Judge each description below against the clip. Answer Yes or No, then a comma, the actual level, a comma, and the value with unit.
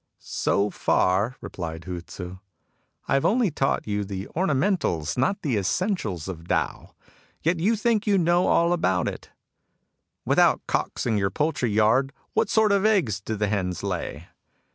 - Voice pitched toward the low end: Yes, low, 110 Hz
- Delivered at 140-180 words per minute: Yes, average, 175 wpm